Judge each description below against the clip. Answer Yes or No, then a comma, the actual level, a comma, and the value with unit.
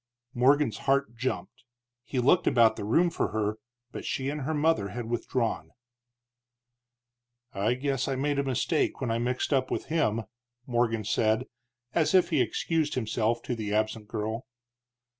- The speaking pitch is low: Yes, low, 125 Hz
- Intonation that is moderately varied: Yes, average, 4.1 semitones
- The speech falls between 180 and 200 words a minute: No, average, 160 wpm